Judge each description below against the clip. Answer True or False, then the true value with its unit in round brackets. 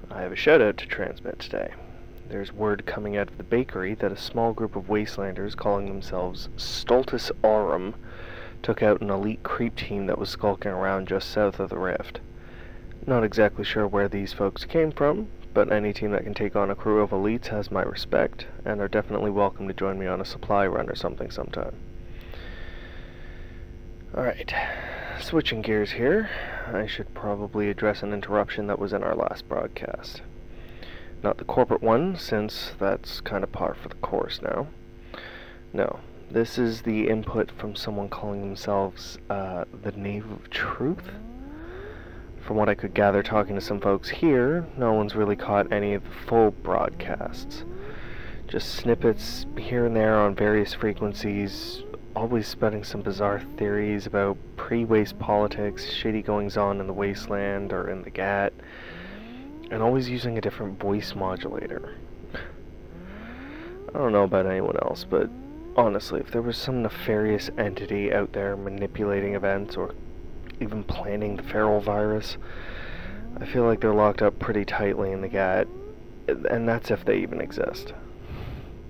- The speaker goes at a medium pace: True (160 wpm)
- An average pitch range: False (2.1 semitones)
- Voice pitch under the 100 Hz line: False (105 Hz)